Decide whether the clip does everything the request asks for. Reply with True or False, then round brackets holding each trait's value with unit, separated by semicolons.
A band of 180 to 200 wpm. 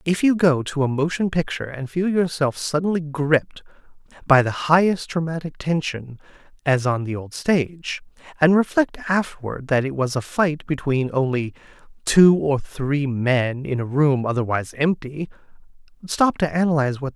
False (170 wpm)